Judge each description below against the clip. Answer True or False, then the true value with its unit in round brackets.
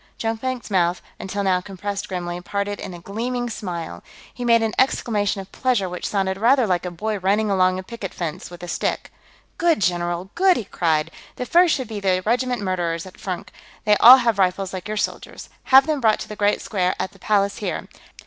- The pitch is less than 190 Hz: False (200 Hz)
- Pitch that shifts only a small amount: False (4.1 semitones)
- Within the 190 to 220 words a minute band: True (205 wpm)